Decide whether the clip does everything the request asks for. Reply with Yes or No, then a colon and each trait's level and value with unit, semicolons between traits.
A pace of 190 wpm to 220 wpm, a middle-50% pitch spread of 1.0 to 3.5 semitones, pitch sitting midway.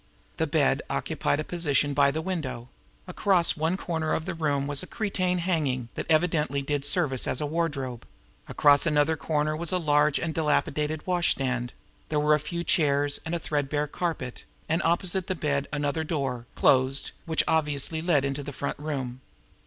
No: average, 175 wpm; average, 2.8 semitones; medium, 150 Hz